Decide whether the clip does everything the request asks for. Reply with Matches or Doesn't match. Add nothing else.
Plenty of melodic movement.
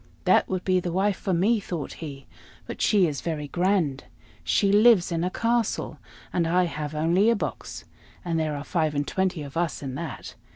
Doesn't match